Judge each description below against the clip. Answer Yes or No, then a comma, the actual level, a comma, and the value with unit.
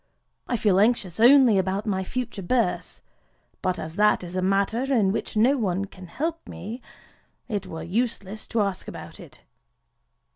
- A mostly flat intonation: No, average, 3.9 semitones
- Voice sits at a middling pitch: No, high, 205 Hz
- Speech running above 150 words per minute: Yes, average, 160 wpm